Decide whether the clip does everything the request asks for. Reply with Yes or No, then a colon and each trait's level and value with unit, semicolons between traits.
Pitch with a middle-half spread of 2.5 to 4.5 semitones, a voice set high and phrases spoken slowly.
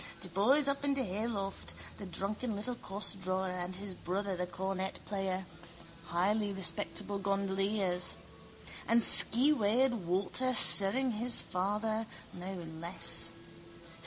Yes: average, 3.0 semitones; high, 200 Hz; slow, 115 wpm